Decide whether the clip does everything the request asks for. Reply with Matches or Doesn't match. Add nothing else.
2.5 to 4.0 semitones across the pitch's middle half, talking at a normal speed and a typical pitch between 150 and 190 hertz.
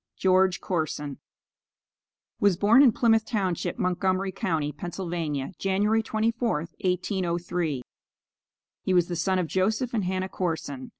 Doesn't match